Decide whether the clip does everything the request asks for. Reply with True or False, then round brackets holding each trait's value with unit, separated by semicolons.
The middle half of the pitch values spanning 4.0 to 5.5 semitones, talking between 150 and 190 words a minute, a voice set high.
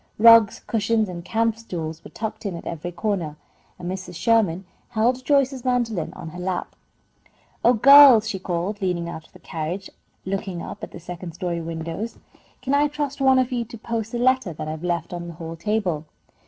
False (5.2 semitones; 200 wpm; 195 Hz)